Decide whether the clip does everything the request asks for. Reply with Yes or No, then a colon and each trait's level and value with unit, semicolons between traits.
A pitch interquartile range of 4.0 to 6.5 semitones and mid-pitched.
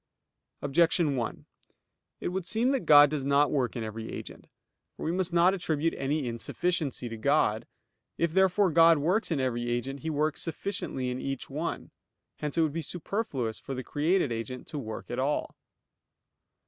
Yes: average, 4.8 semitones; medium, 150 Hz